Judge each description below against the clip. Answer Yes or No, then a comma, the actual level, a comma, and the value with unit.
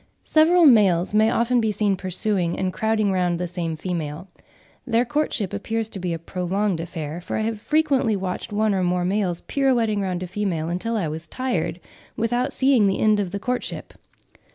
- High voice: Yes, high, 200 Hz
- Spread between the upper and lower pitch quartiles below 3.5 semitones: No, average, 4.2 semitones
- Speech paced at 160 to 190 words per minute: Yes, average, 185 wpm